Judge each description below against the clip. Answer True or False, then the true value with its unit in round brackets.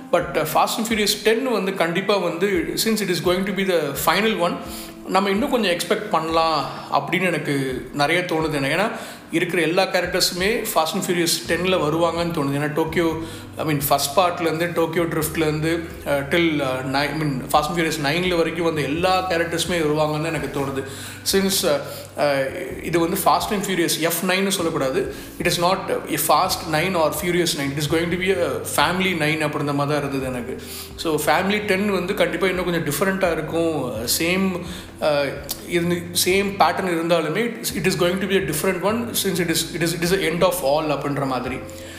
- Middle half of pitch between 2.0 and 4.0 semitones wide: True (3.7 semitones)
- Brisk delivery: True (175 wpm)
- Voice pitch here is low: False (170 Hz)